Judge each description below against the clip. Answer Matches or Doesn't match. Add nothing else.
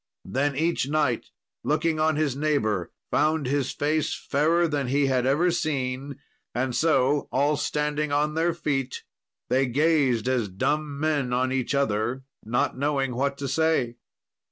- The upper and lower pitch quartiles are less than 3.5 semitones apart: Matches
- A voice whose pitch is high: Doesn't match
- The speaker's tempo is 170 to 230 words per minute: Doesn't match